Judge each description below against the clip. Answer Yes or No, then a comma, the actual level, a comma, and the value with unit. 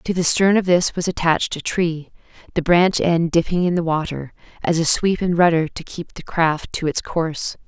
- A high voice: No, medium, 170 Hz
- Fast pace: Yes, fast, 220 wpm